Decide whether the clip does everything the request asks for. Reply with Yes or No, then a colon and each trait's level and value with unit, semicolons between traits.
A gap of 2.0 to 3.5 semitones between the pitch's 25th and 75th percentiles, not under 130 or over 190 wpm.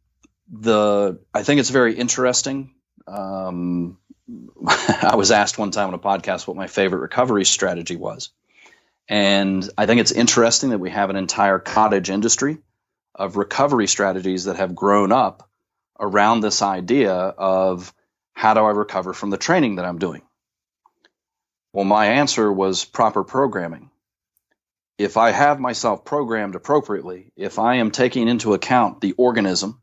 Yes: average, 3.2 semitones; average, 150 wpm